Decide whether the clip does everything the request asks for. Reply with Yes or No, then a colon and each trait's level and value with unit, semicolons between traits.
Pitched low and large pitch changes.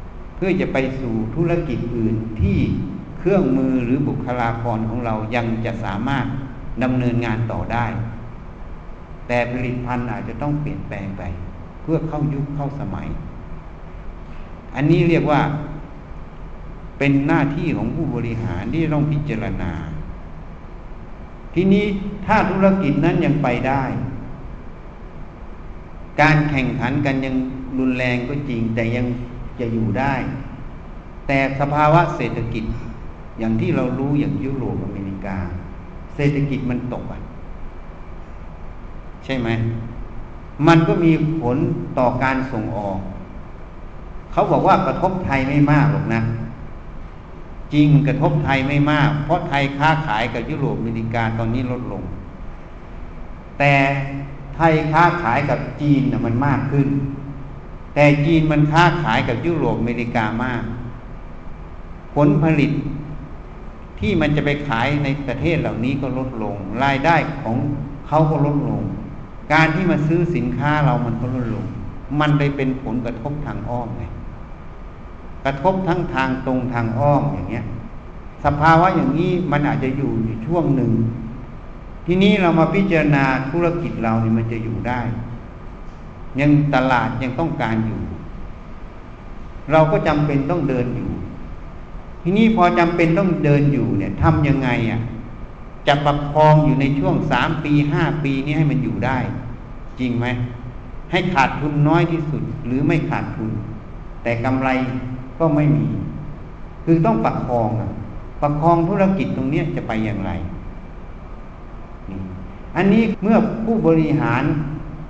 No: low, 130 Hz; average, 4.7 semitones